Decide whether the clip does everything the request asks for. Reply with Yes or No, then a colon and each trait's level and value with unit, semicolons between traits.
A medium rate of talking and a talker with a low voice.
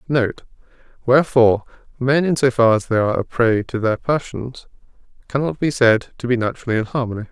Yes: average, 180 wpm; low, 125 Hz